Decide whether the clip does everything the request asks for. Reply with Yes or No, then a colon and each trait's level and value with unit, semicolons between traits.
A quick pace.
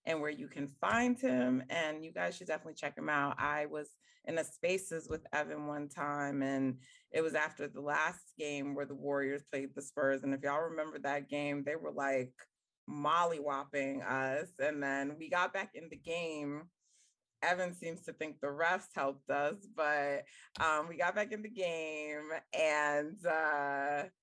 No: average, 185 wpm